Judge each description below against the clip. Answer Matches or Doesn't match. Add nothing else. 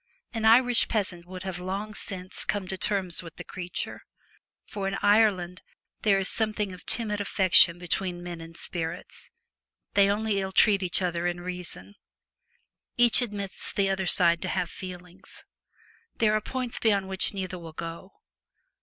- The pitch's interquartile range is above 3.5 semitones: Doesn't match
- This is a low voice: Doesn't match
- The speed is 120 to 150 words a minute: Doesn't match